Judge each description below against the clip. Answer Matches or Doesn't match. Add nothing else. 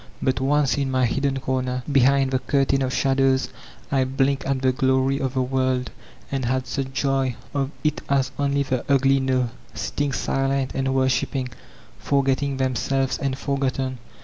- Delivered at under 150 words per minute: Doesn't match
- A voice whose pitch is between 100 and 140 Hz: Matches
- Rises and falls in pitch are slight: Matches